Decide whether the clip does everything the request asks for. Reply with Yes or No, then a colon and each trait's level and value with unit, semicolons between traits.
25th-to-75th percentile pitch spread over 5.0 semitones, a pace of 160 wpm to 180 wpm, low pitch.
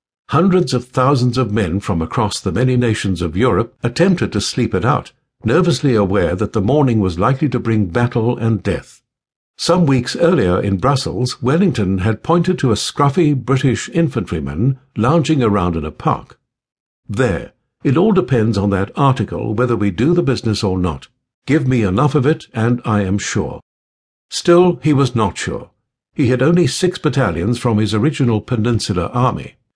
Yes: wide, 5.5 semitones; average, 170 wpm; low, 120 Hz